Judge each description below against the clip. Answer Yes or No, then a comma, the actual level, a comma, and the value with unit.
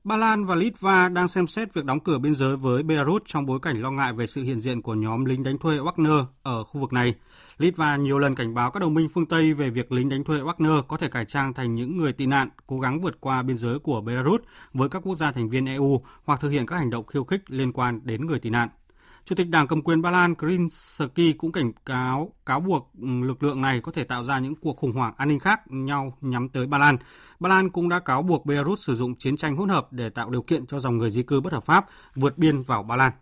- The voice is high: No, medium, 140 Hz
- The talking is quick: Yes, fast, 270 wpm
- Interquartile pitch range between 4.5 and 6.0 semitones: No, average, 4.1 semitones